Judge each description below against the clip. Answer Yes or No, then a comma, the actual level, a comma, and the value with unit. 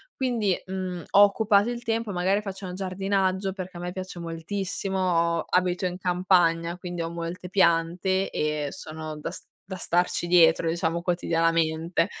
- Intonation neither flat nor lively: No, narrow, 2.3 semitones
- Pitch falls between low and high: Yes, medium, 180 Hz